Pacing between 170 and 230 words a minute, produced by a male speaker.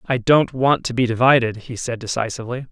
Yes: average, 200 wpm; male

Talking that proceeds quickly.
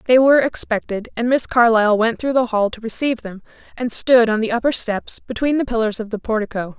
Yes: fast, 220 wpm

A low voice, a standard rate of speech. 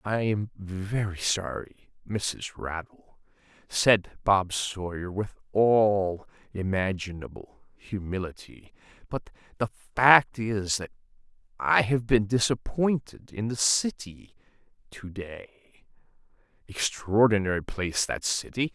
No: low, 105 Hz; slow, 95 wpm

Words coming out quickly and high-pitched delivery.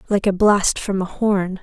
Yes: fast, 220 wpm; high, 195 Hz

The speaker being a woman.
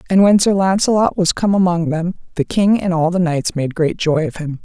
Yes: female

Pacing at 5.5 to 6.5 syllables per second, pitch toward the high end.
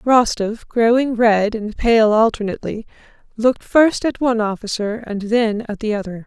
No: 4.8 syllables/s; high, 225 Hz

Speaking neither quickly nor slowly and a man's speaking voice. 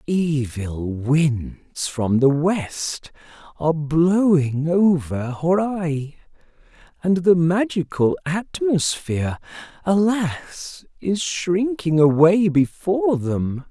No: slow, 85 wpm; male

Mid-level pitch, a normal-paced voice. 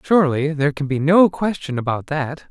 Yes: medium, 150 Hz; average, 190 wpm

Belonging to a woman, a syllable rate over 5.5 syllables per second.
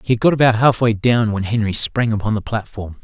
No: male; 5.9 syllables/s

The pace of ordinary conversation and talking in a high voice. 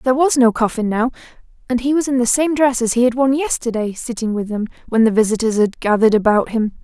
No: fast, 235 wpm; high, 240 Hz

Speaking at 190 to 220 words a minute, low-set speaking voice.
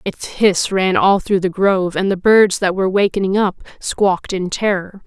No: average, 200 wpm; high, 190 Hz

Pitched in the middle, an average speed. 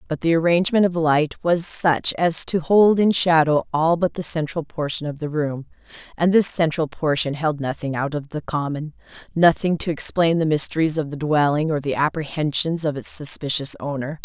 Yes: medium, 155 Hz; average, 185 wpm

